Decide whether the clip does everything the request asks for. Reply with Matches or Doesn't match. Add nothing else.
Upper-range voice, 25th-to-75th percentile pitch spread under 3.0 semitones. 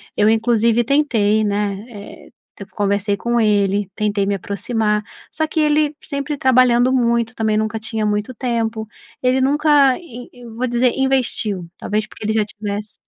Doesn't match